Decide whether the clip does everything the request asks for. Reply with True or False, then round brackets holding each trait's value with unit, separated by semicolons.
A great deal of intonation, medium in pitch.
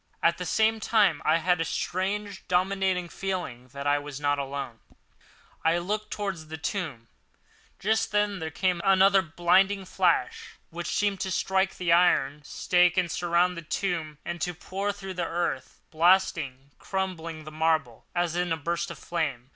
False (3.5 semitones; 175 Hz)